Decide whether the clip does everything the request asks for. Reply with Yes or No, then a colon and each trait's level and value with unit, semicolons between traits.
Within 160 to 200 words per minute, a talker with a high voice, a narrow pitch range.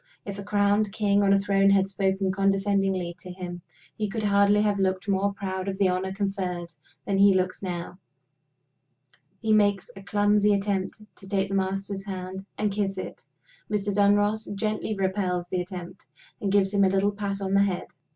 Yes: average, 180 wpm; high, 195 Hz; narrow, 1.2 semitones